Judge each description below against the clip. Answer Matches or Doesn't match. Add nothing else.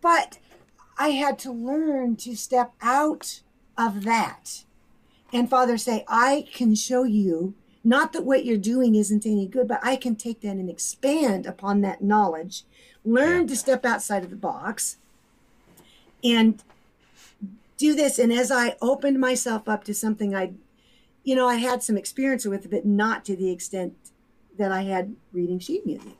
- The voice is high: Matches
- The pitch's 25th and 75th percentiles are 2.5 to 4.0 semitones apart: Matches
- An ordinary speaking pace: Matches